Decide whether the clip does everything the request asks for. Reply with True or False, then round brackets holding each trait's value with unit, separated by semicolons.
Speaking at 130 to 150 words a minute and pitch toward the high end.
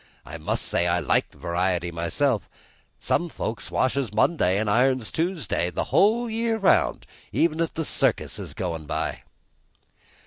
False (145 wpm; 125 Hz)